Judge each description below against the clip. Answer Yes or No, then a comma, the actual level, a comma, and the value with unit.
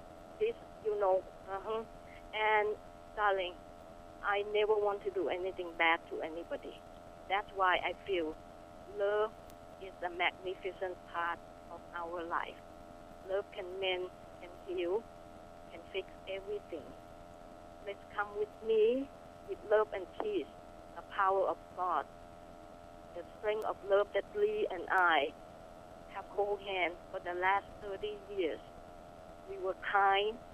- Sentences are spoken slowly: Yes, slow, 130 wpm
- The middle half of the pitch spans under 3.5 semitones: Yes, narrow, 2.4 semitones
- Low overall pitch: No, high, 205 Hz